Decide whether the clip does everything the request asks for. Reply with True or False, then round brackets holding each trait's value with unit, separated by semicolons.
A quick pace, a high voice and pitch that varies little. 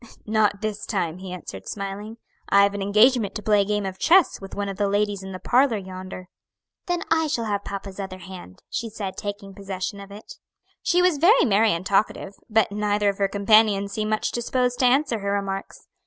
True (210 wpm; 205 Hz; 2.1 semitones)